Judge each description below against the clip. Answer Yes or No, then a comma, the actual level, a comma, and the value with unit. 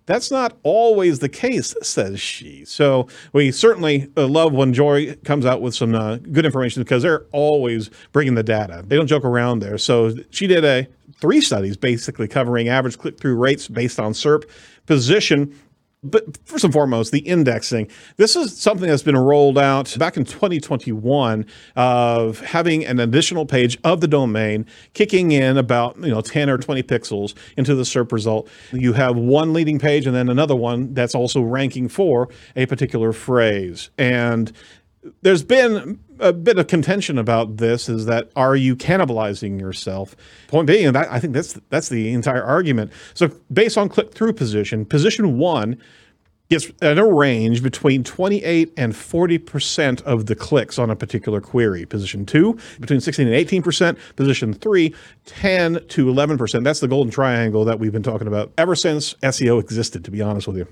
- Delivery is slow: No, average, 175 wpm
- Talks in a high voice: No, low, 130 Hz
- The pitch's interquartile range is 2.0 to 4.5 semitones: No, average, 5.0 semitones